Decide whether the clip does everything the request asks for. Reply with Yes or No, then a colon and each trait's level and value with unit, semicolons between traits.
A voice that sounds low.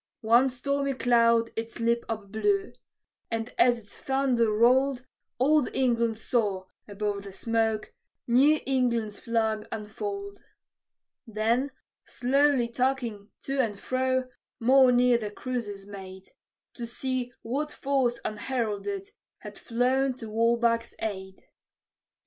No: high, 235 Hz